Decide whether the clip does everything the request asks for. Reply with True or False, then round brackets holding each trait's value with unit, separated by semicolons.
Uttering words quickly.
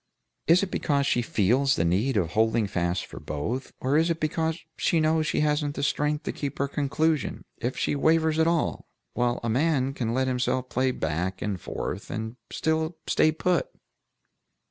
False (190 wpm)